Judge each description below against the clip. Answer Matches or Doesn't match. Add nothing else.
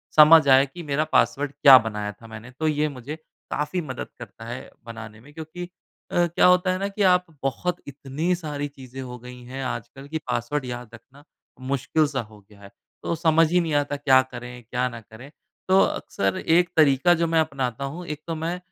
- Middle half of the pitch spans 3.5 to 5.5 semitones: Matches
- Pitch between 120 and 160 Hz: Matches